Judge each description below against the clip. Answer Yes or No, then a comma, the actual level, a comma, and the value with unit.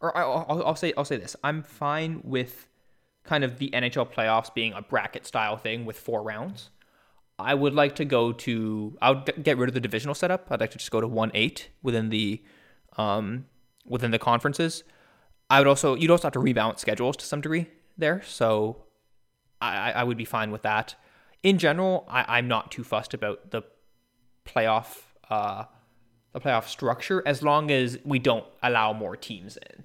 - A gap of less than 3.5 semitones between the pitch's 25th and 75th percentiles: No, average, 4.6 semitones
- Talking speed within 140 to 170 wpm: No, average, 190 wpm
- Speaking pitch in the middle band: No, low, 125 Hz